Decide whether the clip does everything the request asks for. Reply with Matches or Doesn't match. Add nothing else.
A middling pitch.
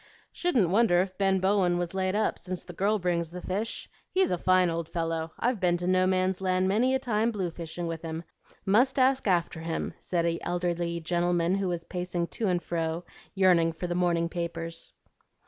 Matches